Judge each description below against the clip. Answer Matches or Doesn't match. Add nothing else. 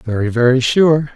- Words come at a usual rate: Matches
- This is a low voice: Matches